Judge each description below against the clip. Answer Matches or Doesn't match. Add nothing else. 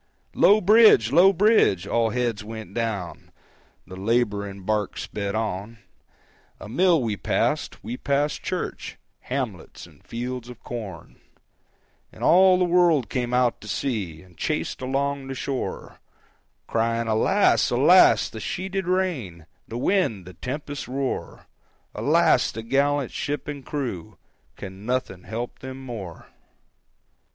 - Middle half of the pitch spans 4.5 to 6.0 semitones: Matches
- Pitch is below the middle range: Matches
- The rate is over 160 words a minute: Doesn't match